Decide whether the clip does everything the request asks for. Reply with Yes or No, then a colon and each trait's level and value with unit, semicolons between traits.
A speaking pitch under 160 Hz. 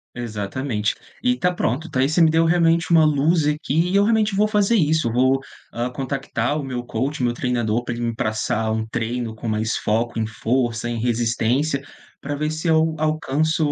Yes: low, 135 Hz